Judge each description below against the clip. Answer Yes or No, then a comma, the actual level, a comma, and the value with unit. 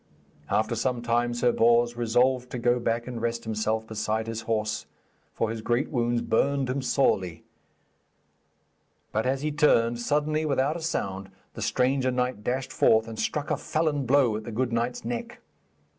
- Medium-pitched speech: No, low, 120 Hz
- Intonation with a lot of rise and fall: No, narrow, 2.6 semitones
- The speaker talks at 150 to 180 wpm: Yes, average, 170 wpm